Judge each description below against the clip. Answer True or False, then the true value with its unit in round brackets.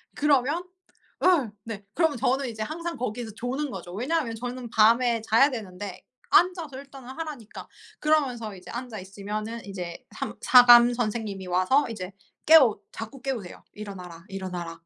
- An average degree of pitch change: True (4.9 semitones)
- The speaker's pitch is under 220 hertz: False (235 Hz)